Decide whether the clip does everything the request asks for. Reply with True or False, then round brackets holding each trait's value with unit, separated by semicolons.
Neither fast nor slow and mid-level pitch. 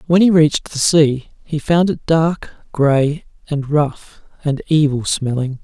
True (160 wpm; 150 Hz)